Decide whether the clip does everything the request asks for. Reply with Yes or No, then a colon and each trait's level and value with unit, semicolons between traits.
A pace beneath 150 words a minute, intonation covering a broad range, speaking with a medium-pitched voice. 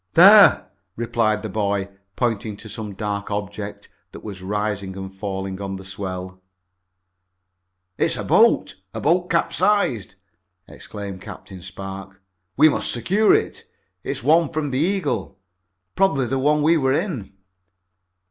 No: slow, 135 wpm; wide, 7.2 semitones; low, 105 Hz